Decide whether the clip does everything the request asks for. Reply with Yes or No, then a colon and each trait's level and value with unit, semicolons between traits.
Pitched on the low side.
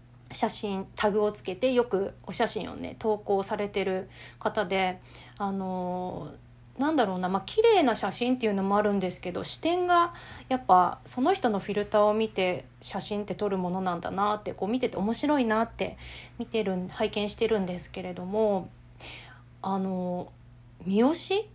No: high, 200 Hz